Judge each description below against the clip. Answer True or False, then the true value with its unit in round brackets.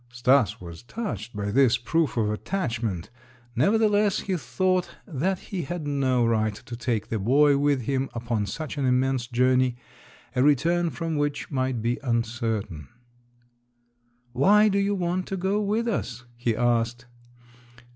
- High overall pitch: False (130 Hz)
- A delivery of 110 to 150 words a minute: True (145 wpm)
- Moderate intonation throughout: False (6.6 semitones)